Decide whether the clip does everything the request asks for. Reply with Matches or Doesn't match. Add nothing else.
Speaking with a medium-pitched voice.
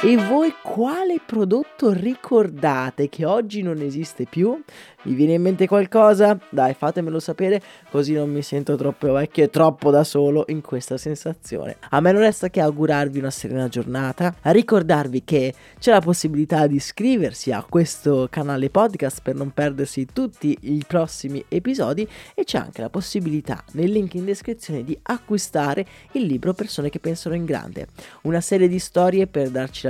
Matches